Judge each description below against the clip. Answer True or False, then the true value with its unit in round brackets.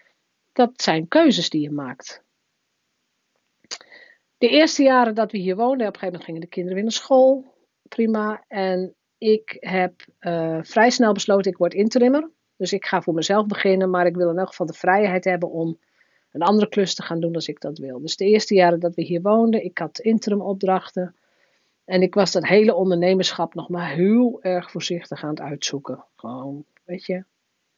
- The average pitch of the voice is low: False (185 Hz)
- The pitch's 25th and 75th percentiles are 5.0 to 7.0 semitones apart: False (3.9 semitones)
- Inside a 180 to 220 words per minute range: True (190 wpm)